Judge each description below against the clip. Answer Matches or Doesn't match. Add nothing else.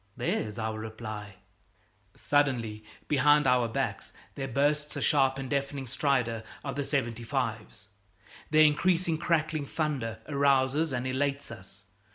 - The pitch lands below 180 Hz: Matches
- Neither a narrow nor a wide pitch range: Matches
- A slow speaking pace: Matches